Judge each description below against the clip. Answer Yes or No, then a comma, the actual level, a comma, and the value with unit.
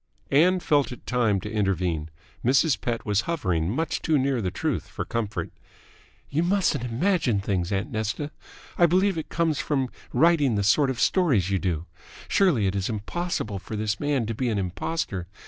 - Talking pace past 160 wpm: Yes, average, 180 wpm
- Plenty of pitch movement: Yes, wide, 7.7 semitones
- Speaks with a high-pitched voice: No, low, 120 Hz